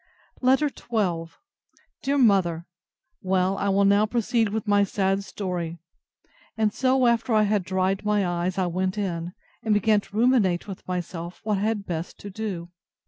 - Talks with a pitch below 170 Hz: No, high, 200 Hz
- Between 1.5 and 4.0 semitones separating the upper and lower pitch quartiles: Yes, average, 3.1 semitones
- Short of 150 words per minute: No, average, 165 wpm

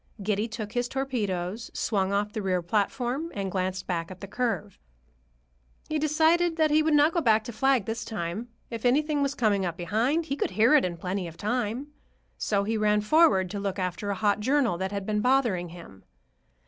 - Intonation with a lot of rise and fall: Yes, wide, 5.8 semitones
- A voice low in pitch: No, high, 215 Hz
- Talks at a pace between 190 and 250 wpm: Yes, average, 200 wpm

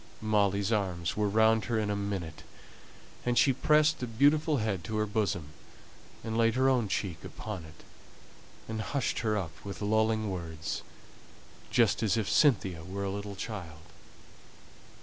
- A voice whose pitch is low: Yes, low, 105 Hz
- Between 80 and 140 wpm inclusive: No, average, 155 wpm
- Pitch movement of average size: Yes, average, 3.0 semitones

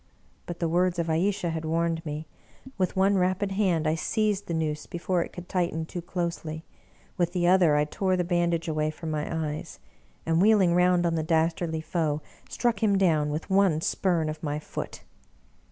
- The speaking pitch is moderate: Yes, medium, 170 Hz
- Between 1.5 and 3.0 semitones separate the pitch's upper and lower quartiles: Yes, narrow, 2.4 semitones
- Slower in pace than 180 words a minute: No, average, 185 wpm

